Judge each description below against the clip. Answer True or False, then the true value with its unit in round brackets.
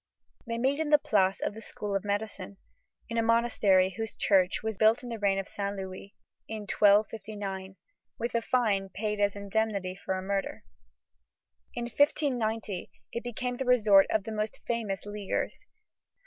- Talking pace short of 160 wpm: False (165 wpm)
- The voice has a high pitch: True (210 Hz)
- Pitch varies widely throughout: False (2.8 semitones)